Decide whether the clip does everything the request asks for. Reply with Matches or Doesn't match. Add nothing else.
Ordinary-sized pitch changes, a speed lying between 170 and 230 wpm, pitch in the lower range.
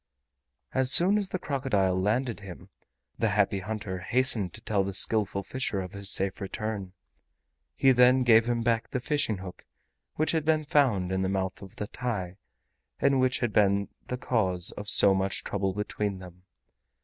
Matches